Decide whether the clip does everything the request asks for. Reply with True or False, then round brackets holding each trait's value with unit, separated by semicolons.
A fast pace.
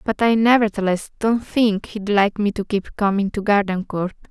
False (180 wpm)